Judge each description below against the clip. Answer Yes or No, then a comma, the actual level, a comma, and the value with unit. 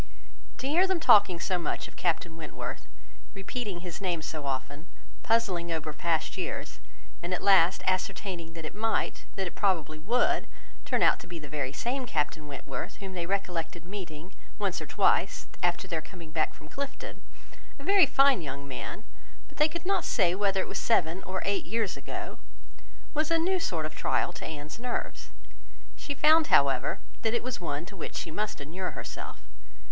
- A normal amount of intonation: No, wide, 6.0 semitones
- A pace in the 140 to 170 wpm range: No, average, 180 wpm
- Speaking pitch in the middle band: Yes, medium, 180 Hz